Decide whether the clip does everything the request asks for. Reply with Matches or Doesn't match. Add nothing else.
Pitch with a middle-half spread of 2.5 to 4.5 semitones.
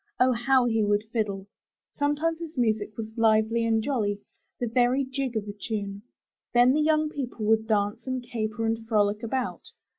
Matches